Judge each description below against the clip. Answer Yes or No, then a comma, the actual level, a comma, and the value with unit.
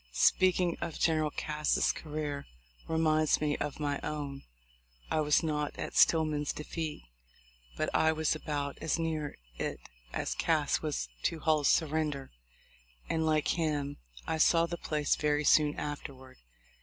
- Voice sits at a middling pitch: Yes, medium, 150 Hz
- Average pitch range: No, narrow, 1.4 semitones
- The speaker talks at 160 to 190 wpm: No, average, 145 wpm